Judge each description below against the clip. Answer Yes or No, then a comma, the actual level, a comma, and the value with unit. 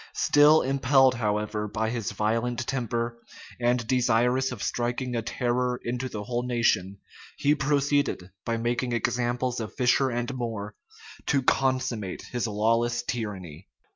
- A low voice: Yes, low, 120 Hz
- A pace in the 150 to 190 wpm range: No, slow, 135 wpm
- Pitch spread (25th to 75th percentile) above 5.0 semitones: No, narrow, 2.4 semitones